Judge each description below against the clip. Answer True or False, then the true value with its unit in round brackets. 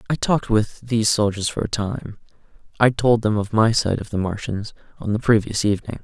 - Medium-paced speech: False (210 wpm)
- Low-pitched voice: True (110 Hz)